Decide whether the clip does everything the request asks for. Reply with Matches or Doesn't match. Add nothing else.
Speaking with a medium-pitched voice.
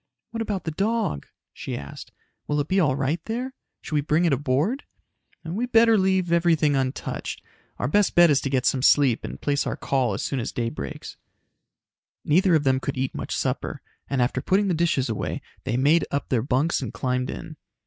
Matches